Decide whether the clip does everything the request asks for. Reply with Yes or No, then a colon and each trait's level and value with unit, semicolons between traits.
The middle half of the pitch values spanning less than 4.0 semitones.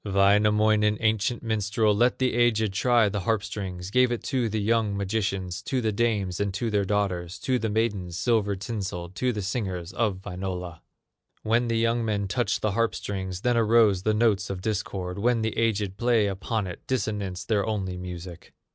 Yes: average, 3.0 semitones